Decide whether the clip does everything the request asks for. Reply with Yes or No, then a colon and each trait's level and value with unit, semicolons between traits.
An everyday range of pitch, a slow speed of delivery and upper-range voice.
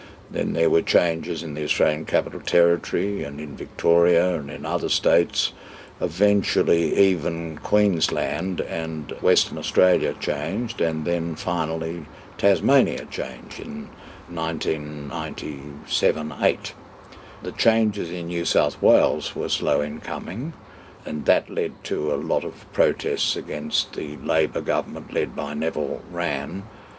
No: average, 3.7 semitones; slow, 125 wpm; very low, 85 Hz